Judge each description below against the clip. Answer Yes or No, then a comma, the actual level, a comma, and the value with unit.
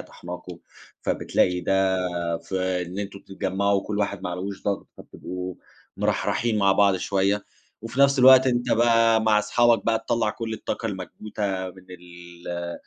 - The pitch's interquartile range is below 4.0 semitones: Yes, average, 3.4 semitones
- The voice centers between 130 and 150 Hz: No, low, 100 Hz